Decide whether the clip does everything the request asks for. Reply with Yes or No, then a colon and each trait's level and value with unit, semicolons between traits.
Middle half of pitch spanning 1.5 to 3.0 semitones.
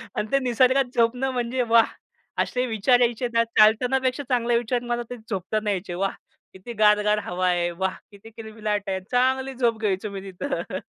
No: average, 3.4 semitones